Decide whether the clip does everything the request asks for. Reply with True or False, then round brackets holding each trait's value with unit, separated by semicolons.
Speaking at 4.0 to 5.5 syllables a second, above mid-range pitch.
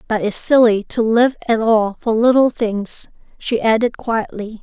True (4.2 syllables/s; 225 Hz)